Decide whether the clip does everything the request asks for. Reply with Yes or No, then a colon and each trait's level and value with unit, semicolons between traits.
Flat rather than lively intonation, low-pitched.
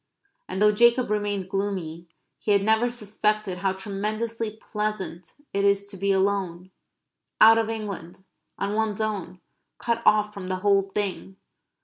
No: narrow, 2.0 semitones; high, 205 Hz